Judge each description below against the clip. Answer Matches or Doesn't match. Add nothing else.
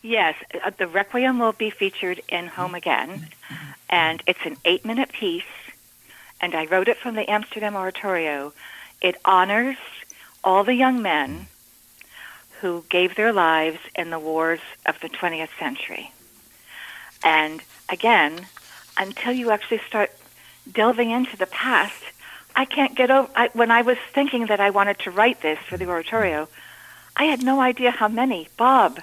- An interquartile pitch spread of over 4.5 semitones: Matches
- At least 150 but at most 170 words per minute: Matches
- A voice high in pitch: Matches